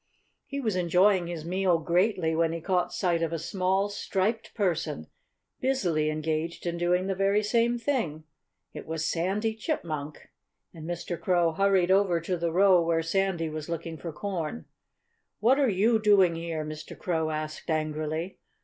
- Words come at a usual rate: Yes, average, 160 wpm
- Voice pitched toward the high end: No, medium, 175 Hz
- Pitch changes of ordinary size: Yes, average, 3.3 semitones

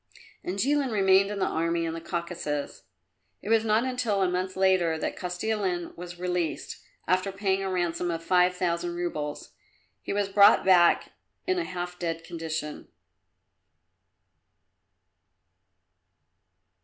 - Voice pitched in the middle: Yes, medium, 180 Hz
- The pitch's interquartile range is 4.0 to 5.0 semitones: No, narrow, 2.6 semitones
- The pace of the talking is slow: Yes, slow, 130 wpm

